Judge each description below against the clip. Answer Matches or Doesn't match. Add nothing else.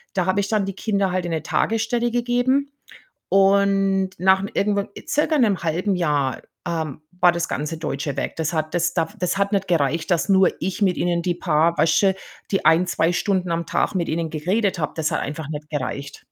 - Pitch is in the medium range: Matches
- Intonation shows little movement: Doesn't match